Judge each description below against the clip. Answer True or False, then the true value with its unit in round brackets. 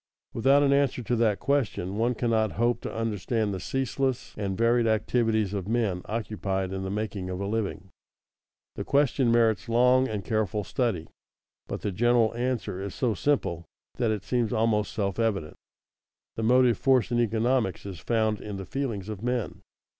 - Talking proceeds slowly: False (170 wpm)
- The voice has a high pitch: False (110 Hz)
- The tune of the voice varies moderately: True (3.2 semitones)